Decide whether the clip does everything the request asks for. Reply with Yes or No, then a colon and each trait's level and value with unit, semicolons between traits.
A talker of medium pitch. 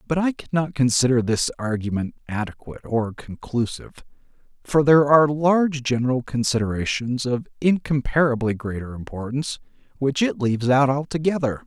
No: low, 130 Hz